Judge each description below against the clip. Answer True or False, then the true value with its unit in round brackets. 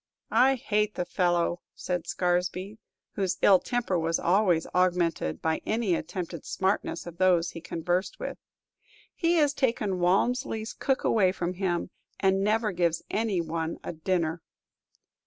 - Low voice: False (185 Hz)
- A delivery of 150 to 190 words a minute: False (140 wpm)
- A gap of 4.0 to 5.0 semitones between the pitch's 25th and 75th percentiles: False (3.6 semitones)